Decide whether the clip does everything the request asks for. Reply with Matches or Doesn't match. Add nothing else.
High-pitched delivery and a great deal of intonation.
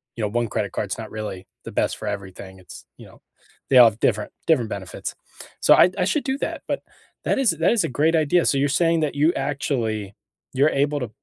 Doesn't match